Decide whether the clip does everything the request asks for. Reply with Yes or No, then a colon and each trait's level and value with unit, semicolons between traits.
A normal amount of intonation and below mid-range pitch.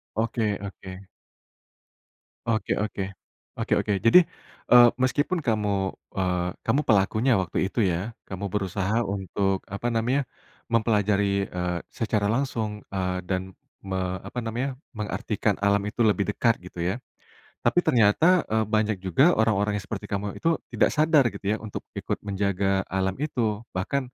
Yes: average, 3.1 semitones; low, 105 Hz